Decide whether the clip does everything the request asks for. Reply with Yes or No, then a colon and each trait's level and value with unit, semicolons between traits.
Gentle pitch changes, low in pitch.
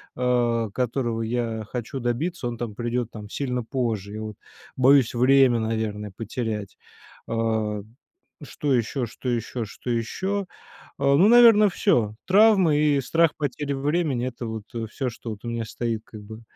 No: average, 3.7 semitones; low, 120 Hz